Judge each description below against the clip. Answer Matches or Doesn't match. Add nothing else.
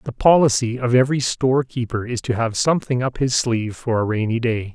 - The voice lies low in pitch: Matches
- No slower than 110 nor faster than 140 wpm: Doesn't match